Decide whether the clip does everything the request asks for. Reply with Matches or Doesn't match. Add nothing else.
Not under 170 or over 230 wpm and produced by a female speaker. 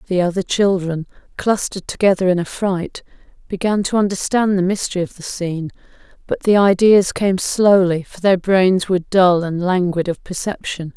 Doesn't match